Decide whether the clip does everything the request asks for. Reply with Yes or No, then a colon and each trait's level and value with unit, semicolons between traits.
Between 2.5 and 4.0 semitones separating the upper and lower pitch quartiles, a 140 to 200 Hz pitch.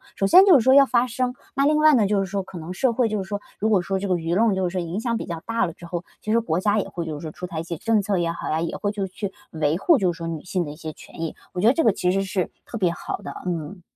No: average, 4.6 semitones; high, 190 Hz